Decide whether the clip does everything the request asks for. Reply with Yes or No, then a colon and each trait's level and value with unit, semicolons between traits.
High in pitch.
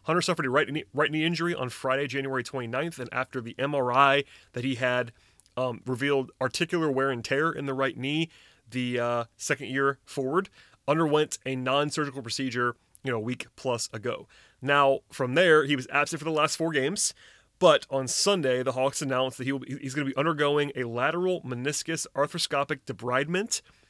No: low, 135 Hz